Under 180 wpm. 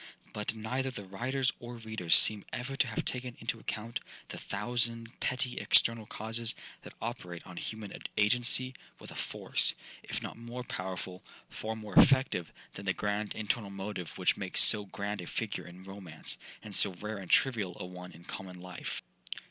Yes: average, 170 wpm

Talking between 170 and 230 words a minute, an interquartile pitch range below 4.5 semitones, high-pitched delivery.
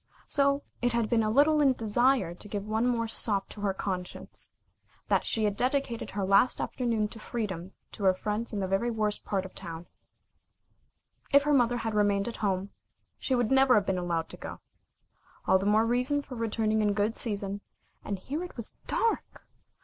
Yes: average, 200 wpm; average, 3.5 semitones; high, 215 Hz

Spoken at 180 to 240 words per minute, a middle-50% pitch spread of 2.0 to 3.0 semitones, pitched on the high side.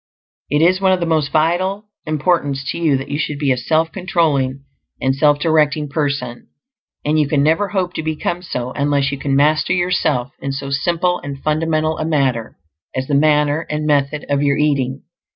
No: average, 190 wpm; narrow, 2.6 semitones; medium, 150 Hz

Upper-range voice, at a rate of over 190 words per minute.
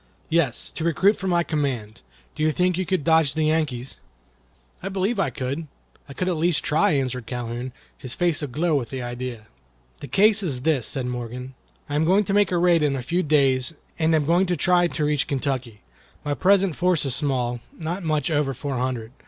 No: medium, 150 Hz; average, 200 wpm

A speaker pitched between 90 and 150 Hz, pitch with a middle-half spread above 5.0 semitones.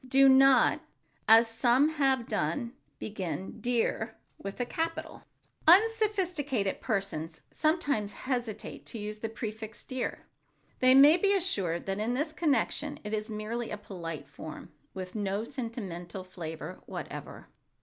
No: high, 225 Hz; wide, 5.6 semitones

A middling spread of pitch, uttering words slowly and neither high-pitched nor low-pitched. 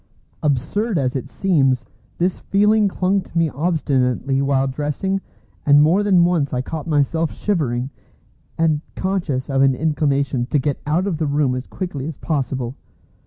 No: average, 4.4 semitones; average, 160 wpm; medium, 150 Hz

